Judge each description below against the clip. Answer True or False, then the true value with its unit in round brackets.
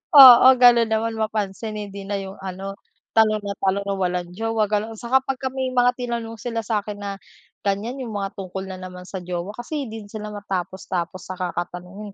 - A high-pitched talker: True (205 Hz)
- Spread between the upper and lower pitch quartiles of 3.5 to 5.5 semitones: False (3.0 semitones)